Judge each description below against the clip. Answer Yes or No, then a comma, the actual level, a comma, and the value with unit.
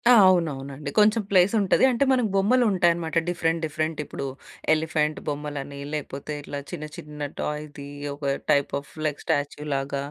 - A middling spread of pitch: Yes, average, 3.6 semitones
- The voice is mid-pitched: Yes, medium, 155 Hz